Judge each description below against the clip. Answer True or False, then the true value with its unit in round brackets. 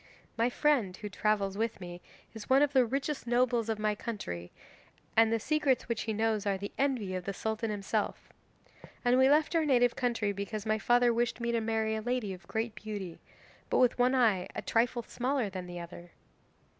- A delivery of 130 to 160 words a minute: False (200 wpm)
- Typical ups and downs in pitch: True (3.3 semitones)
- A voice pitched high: True (225 Hz)